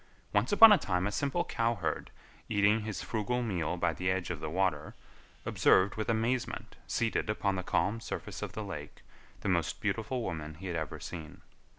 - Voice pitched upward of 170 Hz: No, low, 100 Hz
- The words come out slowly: No, average, 185 wpm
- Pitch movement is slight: No, average, 4.5 semitones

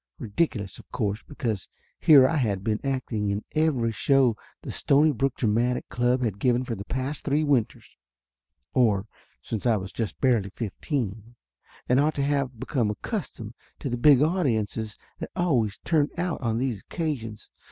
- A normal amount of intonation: Yes, average, 4.4 semitones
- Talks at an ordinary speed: Yes, average, 160 wpm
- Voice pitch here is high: No, low, 125 Hz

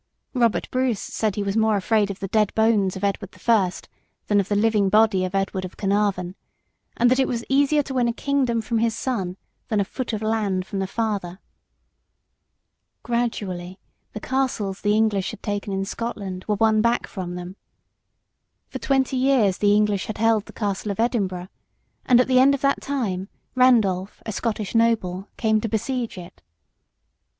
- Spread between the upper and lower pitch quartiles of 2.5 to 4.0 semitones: Yes, average, 3.3 semitones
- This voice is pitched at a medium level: No, high, 215 Hz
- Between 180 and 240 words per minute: Yes, average, 185 wpm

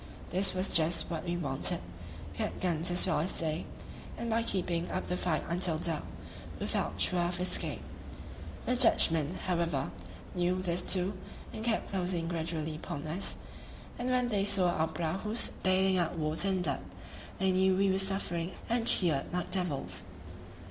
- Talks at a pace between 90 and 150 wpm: No, average, 170 wpm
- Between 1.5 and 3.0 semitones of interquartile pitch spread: Yes, narrow, 2.5 semitones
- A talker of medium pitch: Yes, medium, 180 Hz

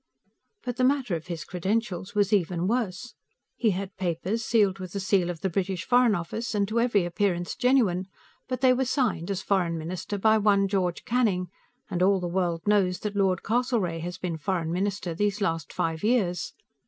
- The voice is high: Yes, high, 195 Hz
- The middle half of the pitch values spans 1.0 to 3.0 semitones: No, average, 3.6 semitones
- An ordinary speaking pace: Yes, average, 190 wpm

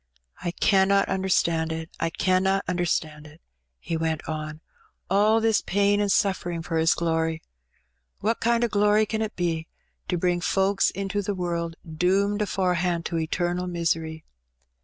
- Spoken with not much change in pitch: No, average, 3.3 semitones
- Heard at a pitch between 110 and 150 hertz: No, medium, 180 Hz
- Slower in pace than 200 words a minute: Yes, average, 160 wpm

